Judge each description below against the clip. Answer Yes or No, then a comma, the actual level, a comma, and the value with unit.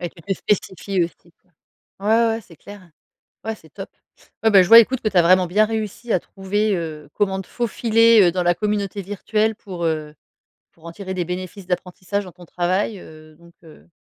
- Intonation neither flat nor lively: Yes, average, 3.3 semitones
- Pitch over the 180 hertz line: Yes, high, 190 Hz